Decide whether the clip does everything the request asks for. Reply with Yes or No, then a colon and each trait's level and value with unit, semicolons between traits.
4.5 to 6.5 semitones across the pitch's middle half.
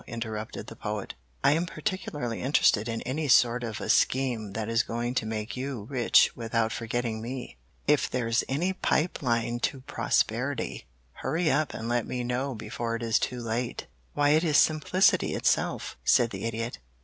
No: average, 3.3 semitones